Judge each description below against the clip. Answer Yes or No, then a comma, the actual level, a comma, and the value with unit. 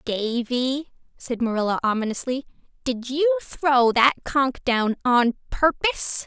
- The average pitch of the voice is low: No, very high, 260 Hz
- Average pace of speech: No, slow, 115 wpm